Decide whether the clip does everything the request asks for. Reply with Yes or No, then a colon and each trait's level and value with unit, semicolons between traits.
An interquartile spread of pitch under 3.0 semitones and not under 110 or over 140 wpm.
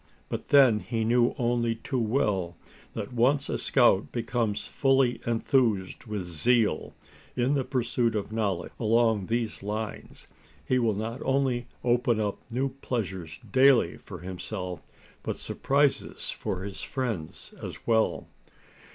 No: average, 3.4 semitones; slow, 135 wpm